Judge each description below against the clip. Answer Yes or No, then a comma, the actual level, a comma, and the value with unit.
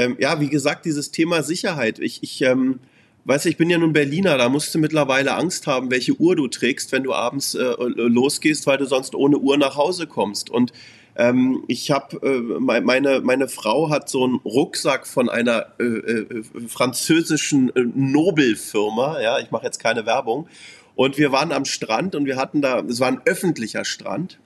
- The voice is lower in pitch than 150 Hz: Yes, low, 135 Hz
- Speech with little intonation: No, average, 3.3 semitones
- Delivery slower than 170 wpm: No, fast, 190 wpm